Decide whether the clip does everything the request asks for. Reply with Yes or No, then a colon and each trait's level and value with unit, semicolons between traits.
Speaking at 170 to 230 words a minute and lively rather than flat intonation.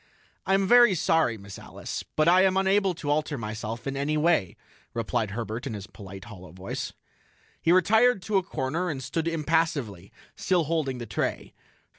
Yes: average, 175 wpm; wide, 8.1 semitones